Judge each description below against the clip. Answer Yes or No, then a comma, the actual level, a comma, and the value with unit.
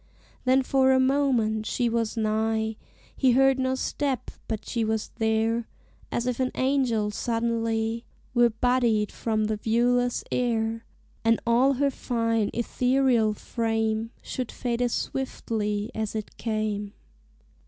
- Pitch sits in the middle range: No, high, 230 Hz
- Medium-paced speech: No, slow, 130 wpm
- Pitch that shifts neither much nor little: No, narrow, 2.3 semitones